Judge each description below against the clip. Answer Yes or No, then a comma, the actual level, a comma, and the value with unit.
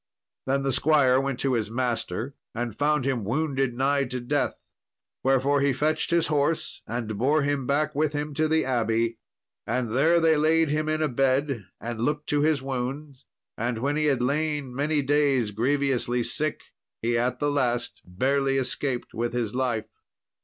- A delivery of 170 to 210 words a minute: Yes, average, 175 wpm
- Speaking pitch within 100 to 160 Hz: Yes, low, 135 Hz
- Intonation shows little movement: No, average, 3.3 semitones